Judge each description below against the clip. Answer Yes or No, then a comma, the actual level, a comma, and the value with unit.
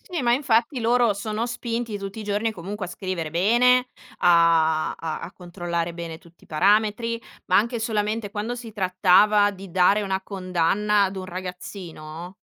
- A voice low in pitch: No, high, 200 Hz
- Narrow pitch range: No, average, 3.9 semitones